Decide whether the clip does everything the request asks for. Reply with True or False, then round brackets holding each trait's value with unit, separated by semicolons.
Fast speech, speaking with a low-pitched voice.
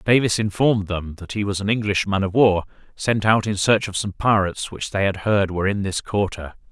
True (230 wpm; 100 Hz)